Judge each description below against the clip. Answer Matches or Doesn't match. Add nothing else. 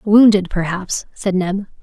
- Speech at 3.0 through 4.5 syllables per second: Matches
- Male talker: Doesn't match